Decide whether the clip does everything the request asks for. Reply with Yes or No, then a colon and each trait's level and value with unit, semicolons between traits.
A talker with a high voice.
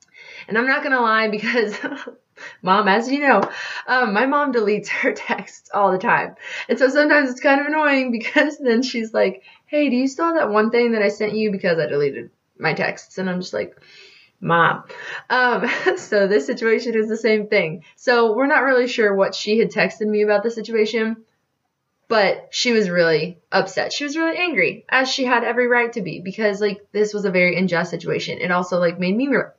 Yes: high, 225 Hz